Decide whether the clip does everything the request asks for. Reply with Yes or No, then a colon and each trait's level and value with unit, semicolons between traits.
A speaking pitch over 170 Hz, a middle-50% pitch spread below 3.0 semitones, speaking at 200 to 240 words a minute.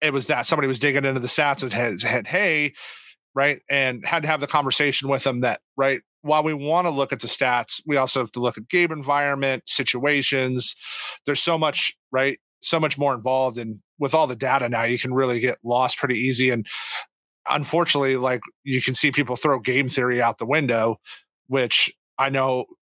No: low, 135 Hz; narrow, 2.5 semitones; fast, 205 wpm